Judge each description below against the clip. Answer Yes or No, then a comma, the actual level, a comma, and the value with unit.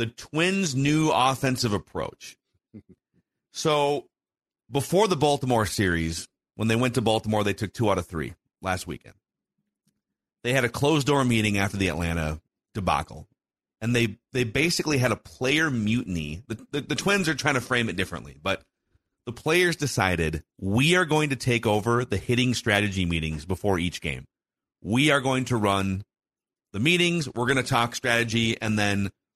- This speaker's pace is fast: No, average, 170 wpm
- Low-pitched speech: Yes, low, 115 Hz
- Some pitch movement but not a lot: No, wide, 5.8 semitones